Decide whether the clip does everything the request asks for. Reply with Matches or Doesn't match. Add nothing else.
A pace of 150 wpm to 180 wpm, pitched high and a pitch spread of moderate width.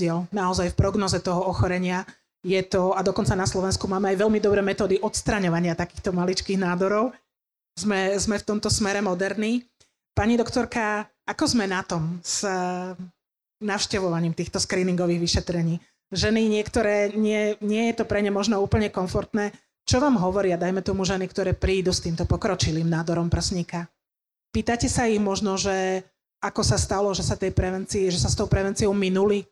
Doesn't match